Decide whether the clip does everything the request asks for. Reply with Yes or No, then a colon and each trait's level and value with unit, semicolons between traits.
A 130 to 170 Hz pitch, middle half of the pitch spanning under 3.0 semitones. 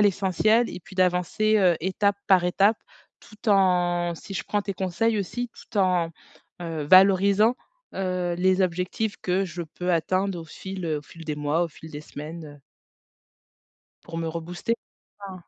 No: medium, 185 Hz; narrow, 2.6 semitones